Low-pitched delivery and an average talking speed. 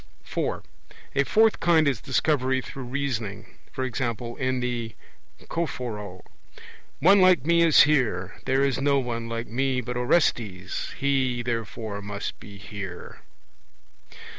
No: low, 125 Hz; slow, 125 wpm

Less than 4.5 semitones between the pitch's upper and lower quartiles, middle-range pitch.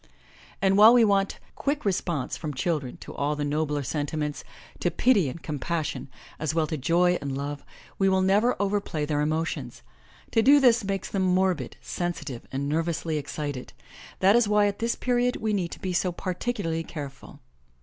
No: average, 5.2 semitones; medium, 170 Hz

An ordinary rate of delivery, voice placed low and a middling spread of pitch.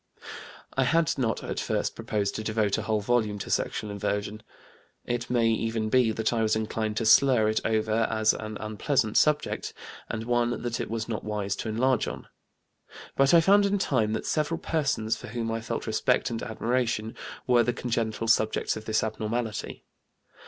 No: average, 180 wpm; low, 115 Hz; narrow, 2.0 semitones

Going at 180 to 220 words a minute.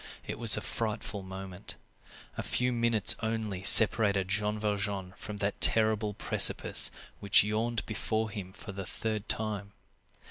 No: average, 140 wpm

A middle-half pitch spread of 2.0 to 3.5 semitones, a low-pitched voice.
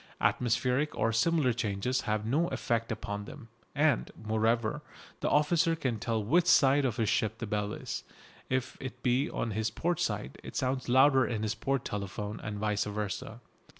No: average, 3.9 semitones; low, 115 Hz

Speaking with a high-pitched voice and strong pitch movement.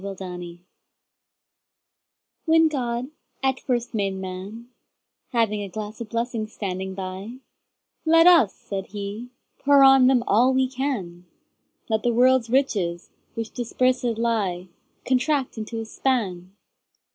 No: high, 230 Hz; average, 4.8 semitones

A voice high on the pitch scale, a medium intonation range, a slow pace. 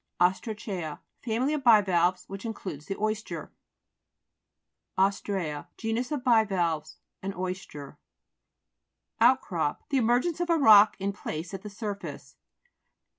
Yes: high, 200 Hz; average, 4.1 semitones; slow, 115 wpm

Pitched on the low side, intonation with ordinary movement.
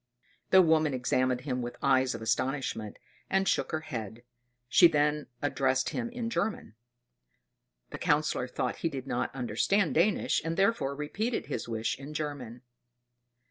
No: medium, 145 Hz; average, 4.7 semitones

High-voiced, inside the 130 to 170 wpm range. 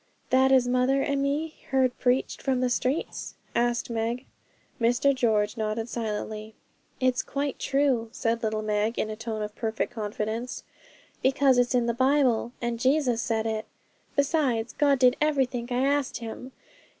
Yes: high, 245 Hz; average, 155 wpm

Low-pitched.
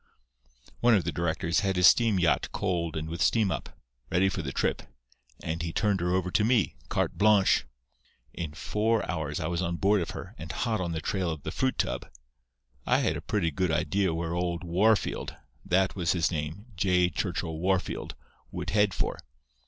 Yes: very low, 90 Hz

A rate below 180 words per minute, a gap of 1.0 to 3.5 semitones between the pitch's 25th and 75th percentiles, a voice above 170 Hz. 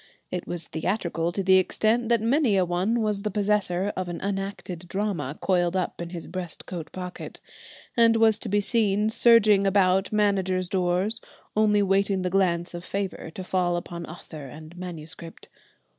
Yes: average, 170 wpm; average, 2.8 semitones; high, 190 Hz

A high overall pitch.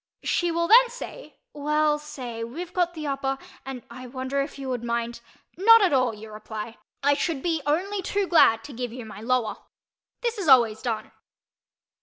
Yes: very high, 275 Hz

